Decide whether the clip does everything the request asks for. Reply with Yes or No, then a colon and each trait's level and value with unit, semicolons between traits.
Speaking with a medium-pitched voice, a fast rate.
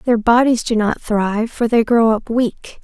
No: high, 230 Hz; fast, 210 wpm